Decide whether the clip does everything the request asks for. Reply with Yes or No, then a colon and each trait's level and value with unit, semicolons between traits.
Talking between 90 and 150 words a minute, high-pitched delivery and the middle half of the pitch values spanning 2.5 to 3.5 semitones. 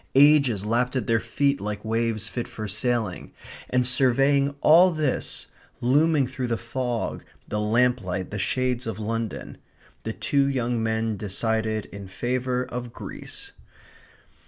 No: slow, 135 wpm; low, 120 Hz; average, 2.8 semitones